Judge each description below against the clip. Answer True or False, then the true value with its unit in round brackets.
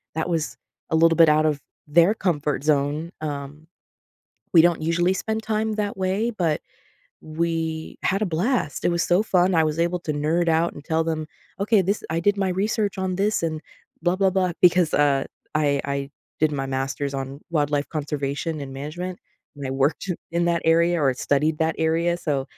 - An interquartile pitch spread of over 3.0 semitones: True (3.4 semitones)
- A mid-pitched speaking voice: True (165 Hz)